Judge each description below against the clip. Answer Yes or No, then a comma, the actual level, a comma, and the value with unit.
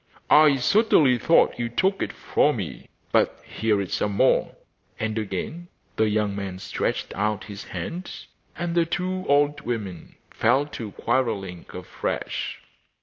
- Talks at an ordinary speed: Yes, average, 145 wpm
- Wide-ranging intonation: Yes, wide, 7.1 semitones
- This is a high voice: No, low, 120 Hz